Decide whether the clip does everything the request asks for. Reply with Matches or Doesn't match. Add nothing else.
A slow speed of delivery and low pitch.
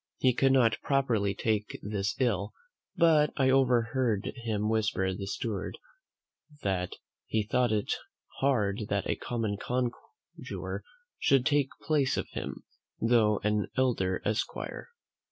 Matches